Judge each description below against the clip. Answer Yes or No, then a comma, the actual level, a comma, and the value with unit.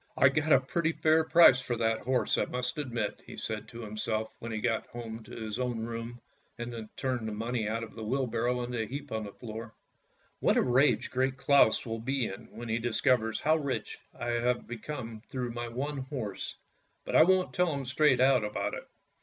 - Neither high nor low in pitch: No, low, 120 Hz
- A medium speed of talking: No, fast, 220 wpm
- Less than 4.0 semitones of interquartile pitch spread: Yes, average, 2.9 semitones